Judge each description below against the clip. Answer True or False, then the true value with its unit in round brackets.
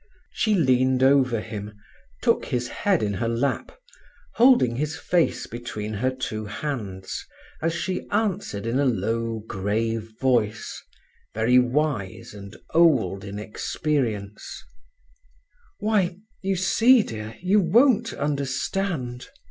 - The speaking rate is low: True (115 wpm)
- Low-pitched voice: True (130 Hz)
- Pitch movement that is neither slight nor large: False (7.6 semitones)